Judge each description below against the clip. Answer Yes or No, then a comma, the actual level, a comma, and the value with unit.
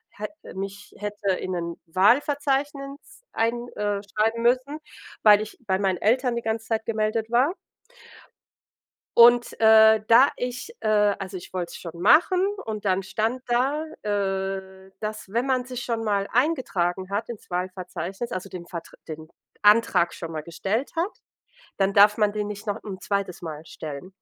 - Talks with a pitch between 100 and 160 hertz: No, high, 210 Hz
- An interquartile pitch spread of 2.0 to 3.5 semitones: No, average, 3.9 semitones